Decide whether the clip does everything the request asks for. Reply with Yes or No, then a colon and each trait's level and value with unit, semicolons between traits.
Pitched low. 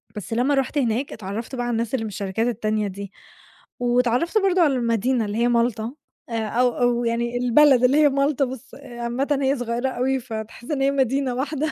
No: high, 245 Hz